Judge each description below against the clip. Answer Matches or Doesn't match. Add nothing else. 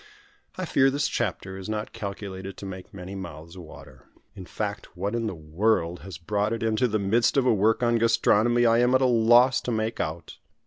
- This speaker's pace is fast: Matches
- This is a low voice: Matches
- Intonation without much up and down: Doesn't match